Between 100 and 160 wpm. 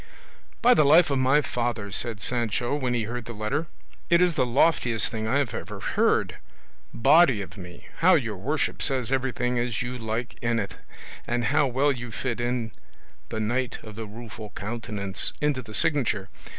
No: average, 175 wpm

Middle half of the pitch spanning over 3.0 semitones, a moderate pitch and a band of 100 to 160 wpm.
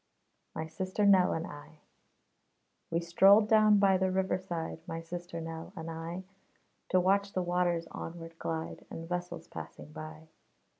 No: narrow, 2.5 semitones; medium, 175 Hz; average, 150 wpm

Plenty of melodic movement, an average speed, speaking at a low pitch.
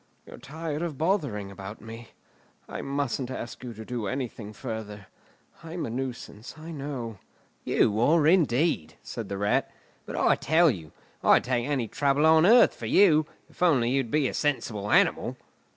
Yes: wide, 5.7 semitones; average, 170 wpm; low, 130 Hz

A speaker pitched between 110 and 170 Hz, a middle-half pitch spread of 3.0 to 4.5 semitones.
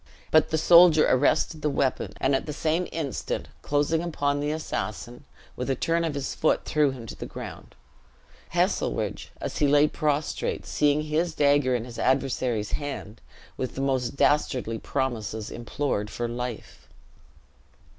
Yes: medium, 140 Hz; average, 3.5 semitones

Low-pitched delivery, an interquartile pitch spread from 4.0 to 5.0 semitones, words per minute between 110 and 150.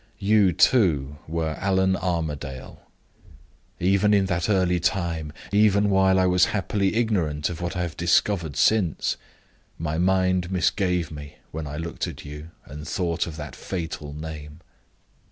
No: very low, 85 Hz; average, 3.6 semitones; average, 145 wpm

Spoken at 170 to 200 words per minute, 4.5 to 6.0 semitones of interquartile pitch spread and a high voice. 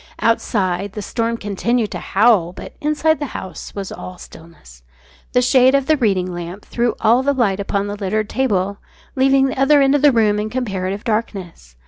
Yes: average, 185 wpm; average, 5.2 semitones; high, 215 Hz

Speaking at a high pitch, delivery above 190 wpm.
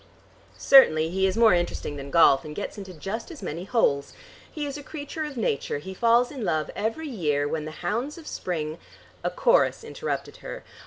Yes: high, 195 Hz; average, 200 wpm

